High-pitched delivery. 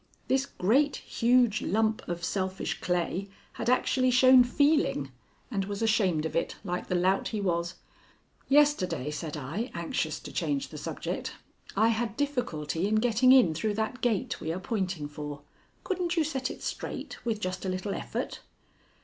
Yes: high, 210 Hz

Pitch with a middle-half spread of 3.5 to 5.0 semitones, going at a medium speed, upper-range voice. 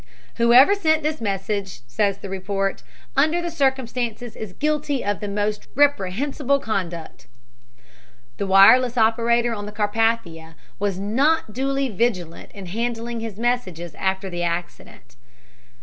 No: average, 4.7 semitones; slow, 130 wpm; high, 220 Hz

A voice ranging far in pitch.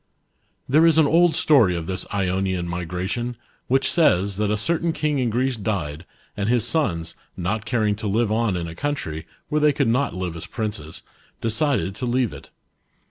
Yes: wide, 6.6 semitones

